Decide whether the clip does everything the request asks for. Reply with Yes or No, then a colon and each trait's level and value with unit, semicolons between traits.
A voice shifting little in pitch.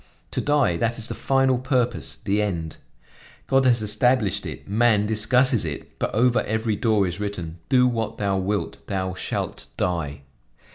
No: average, 4.1 semitones